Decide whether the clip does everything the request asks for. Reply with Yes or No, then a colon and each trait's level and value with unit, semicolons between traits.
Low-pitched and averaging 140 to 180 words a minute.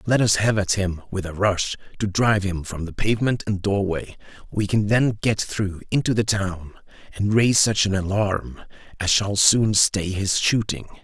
No: low, 100 Hz; average, 190 wpm